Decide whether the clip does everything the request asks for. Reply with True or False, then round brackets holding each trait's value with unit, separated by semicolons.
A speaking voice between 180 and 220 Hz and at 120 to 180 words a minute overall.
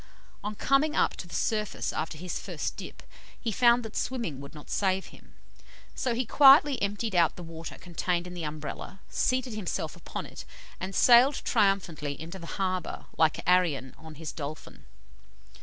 True (185 Hz; 170 wpm)